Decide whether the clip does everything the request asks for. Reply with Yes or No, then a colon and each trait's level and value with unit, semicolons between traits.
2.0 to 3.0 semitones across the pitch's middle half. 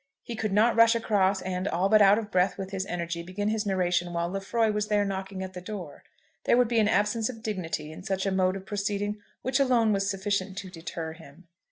Yes: narrow, 2.5 semitones